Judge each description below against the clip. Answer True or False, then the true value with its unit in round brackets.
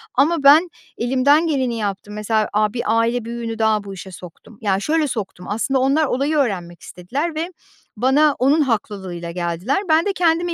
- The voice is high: True (235 Hz)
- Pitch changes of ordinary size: False (6.1 semitones)